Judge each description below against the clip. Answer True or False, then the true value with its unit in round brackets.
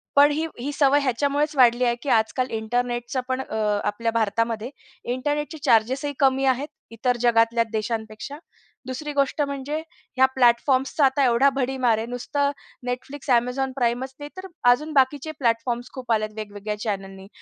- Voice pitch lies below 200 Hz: False (255 Hz)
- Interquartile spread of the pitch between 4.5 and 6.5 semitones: False (3.3 semitones)